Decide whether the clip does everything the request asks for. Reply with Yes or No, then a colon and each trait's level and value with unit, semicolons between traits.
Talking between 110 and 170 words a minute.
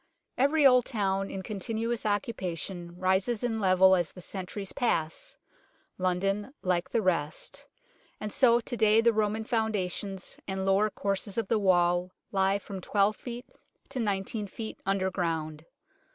Yes: average, 150 wpm